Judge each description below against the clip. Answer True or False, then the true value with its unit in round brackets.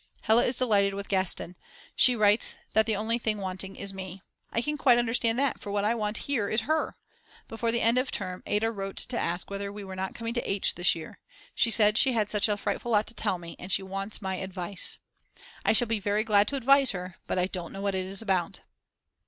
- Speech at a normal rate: False (235 wpm)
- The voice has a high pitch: True (205 Hz)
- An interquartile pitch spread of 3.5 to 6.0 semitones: False (3.1 semitones)